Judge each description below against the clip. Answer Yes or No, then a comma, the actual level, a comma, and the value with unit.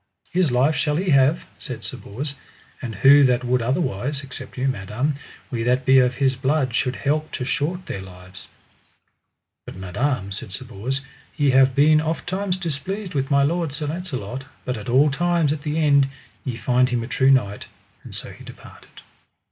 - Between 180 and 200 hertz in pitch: No, low, 135 Hz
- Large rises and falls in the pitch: No, average, 3.3 semitones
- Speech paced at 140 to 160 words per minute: No, average, 190 wpm